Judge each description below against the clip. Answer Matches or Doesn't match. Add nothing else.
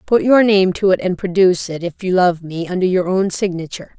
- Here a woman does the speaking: Matches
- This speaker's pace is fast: Matches